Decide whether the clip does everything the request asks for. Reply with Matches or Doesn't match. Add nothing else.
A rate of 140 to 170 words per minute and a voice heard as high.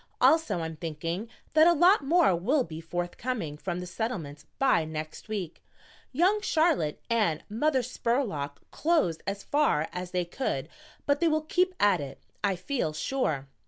Matches